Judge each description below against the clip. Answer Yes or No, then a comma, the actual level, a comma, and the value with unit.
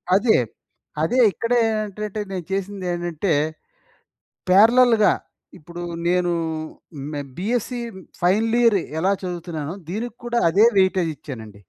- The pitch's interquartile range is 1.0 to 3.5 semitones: No, average, 4.2 semitones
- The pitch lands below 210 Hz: Yes, high, 190 Hz